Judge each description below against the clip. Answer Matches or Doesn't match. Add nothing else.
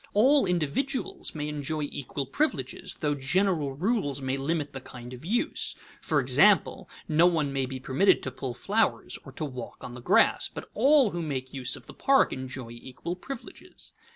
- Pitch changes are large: Matches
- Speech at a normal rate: Matches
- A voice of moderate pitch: Matches